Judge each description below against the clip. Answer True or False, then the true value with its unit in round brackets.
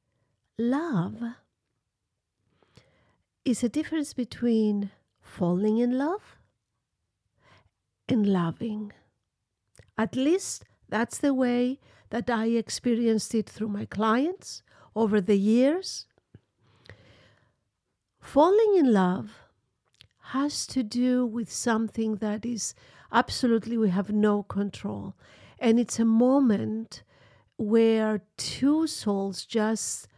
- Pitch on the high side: True (220 Hz)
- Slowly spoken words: True (95 wpm)